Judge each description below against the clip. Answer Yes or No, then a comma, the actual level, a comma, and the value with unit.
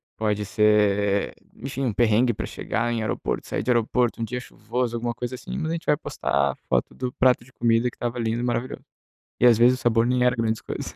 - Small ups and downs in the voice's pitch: Yes, narrow, 2.1 semitones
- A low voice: Yes, low, 120 Hz